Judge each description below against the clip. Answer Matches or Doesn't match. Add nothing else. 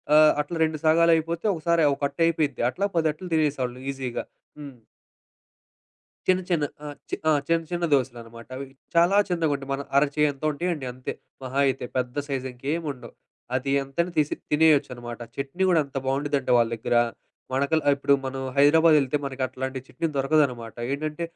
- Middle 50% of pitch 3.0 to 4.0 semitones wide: Matches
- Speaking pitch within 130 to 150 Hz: Matches